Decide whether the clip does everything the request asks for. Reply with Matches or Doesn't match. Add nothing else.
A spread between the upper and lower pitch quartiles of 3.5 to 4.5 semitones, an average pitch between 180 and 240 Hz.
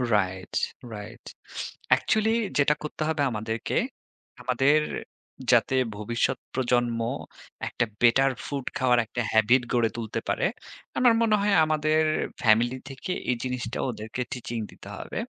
Doesn't match